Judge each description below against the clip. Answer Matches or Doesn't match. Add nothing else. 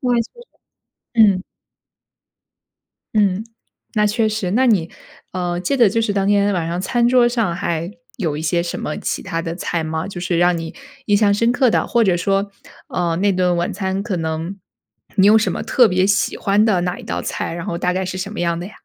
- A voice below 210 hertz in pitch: Matches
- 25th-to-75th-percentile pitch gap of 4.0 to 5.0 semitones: Doesn't match